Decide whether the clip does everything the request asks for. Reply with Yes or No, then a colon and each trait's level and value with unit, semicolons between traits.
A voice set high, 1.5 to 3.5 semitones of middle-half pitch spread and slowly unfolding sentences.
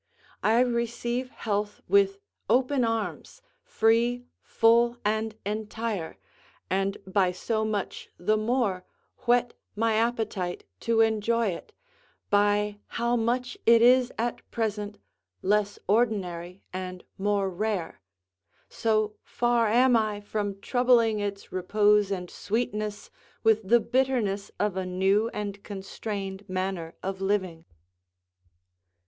Yes: high, 215 Hz; average, 2.9 semitones; slow, 115 wpm